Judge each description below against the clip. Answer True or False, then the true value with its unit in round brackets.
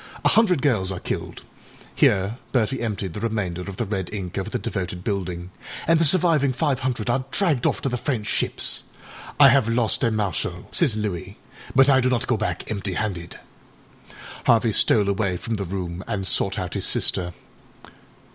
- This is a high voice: False (110 Hz)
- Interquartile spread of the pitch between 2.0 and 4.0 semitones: False (5.3 semitones)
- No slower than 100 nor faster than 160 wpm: False (175 wpm)